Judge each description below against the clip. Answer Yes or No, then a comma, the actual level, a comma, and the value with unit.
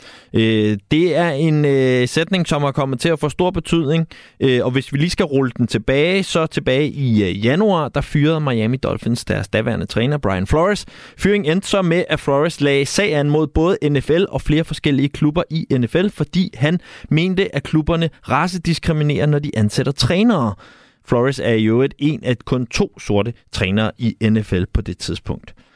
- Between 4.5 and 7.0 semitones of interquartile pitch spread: Yes, average, 5.1 semitones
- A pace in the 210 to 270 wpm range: No, average, 175 wpm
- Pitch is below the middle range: No, medium, 145 Hz